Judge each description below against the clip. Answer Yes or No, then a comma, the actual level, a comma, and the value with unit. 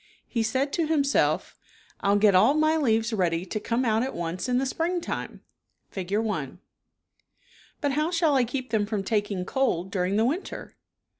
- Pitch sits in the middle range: No, high, 225 Hz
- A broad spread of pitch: Yes, wide, 5.7 semitones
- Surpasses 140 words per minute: Yes, average, 175 wpm